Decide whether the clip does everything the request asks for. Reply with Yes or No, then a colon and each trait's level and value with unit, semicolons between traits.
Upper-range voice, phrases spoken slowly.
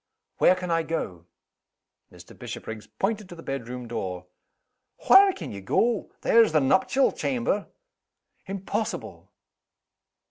No: medium, 170 Hz; slow, 115 wpm